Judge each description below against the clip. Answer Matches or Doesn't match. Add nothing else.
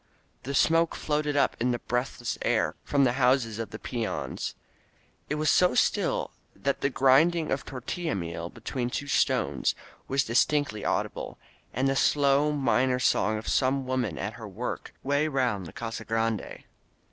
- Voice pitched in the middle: Doesn't match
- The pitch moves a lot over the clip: Doesn't match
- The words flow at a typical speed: Matches